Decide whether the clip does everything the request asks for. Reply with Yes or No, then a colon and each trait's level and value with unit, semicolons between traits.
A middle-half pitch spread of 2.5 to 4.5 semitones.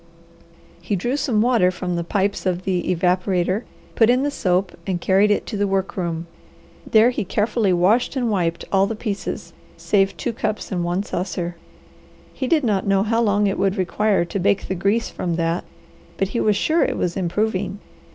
Yes: average, 3.1 semitones